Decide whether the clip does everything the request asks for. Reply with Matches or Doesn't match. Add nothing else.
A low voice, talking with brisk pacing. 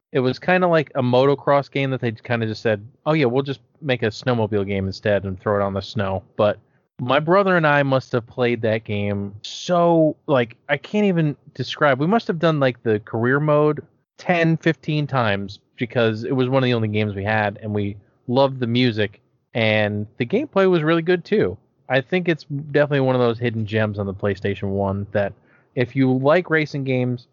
Matches